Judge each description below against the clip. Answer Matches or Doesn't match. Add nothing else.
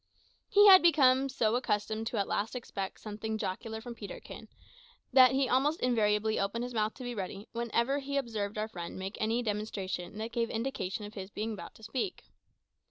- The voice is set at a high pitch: Matches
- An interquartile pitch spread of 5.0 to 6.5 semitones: Doesn't match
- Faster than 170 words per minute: Matches